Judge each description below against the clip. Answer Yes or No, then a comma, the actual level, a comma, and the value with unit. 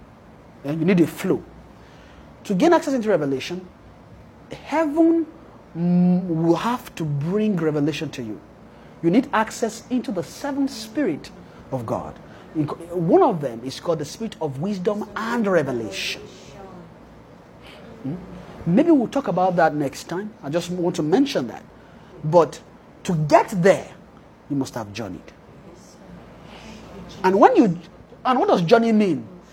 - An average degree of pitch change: No, wide, 6.7 semitones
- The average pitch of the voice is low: No, medium, 180 Hz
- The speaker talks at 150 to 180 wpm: No, slow, 135 wpm